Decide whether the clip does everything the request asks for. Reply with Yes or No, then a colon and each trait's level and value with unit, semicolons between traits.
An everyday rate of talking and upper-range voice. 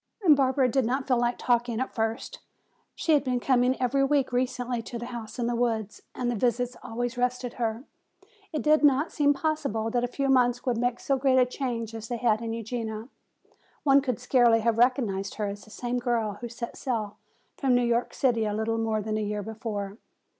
No: fast, 210 wpm; high, 240 Hz